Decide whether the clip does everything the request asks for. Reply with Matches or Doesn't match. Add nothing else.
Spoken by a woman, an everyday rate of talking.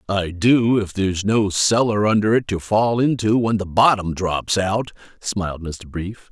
Doesn't match